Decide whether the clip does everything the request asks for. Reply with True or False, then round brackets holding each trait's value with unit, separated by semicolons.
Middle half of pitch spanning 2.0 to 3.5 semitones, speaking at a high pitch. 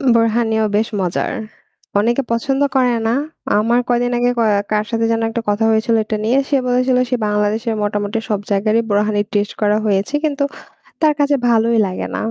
True (2.7 semitones; 225 Hz)